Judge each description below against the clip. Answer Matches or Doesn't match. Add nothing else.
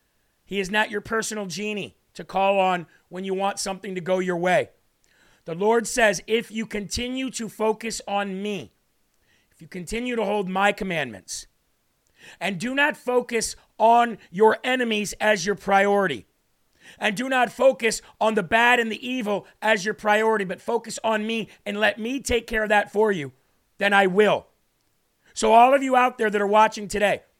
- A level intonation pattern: Matches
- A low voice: Doesn't match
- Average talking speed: Matches